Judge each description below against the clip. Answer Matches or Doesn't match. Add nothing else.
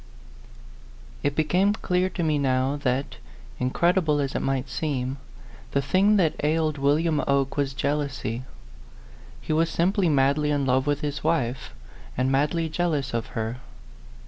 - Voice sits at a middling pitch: Matches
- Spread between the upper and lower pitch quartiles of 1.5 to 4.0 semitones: Matches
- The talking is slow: Doesn't match